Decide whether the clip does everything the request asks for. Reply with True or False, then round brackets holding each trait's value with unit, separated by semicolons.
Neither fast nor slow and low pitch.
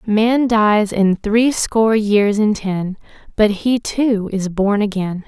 False (160 wpm; 210 Hz)